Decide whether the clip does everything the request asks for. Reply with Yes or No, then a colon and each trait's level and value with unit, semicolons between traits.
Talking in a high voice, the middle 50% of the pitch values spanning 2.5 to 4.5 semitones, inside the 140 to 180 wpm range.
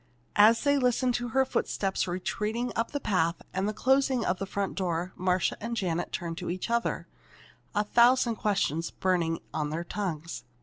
No: high, 195 Hz; average, 5.2 semitones; average, 175 wpm